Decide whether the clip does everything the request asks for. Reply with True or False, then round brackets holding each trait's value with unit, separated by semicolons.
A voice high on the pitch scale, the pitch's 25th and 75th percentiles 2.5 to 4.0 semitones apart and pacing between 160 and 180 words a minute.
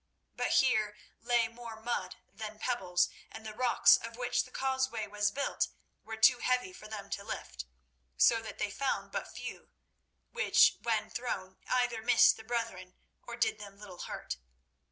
True (220 Hz; 2.8 semitones; 165 wpm)